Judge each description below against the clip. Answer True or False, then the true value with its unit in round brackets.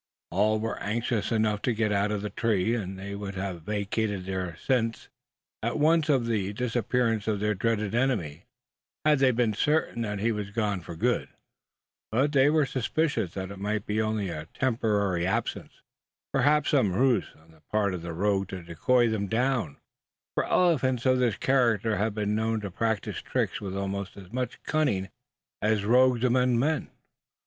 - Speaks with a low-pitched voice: True (110 Hz)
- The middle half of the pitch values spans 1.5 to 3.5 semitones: False (3.9 semitones)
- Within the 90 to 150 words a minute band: False (170 wpm)